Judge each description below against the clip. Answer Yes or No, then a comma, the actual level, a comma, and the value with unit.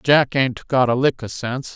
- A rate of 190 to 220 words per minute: No, fast, 240 wpm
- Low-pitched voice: Yes, low, 130 Hz